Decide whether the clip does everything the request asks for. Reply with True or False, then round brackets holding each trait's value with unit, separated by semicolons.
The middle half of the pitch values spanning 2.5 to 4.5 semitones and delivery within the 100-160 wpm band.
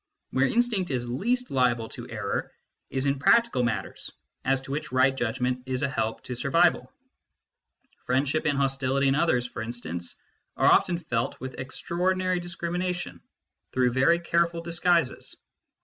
False (5.3 semitones; 145 wpm)